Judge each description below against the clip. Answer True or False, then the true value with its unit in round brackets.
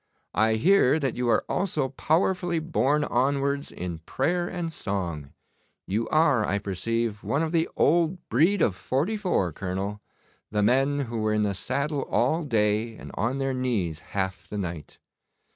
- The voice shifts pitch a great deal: True (7.0 semitones)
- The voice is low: True (125 Hz)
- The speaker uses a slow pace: False (160 wpm)